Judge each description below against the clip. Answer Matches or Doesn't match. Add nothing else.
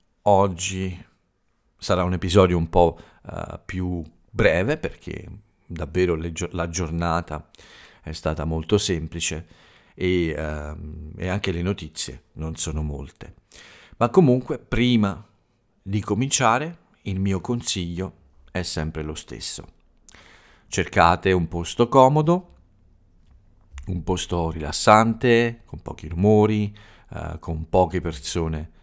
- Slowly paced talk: Matches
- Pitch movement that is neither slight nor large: Matches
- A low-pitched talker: Matches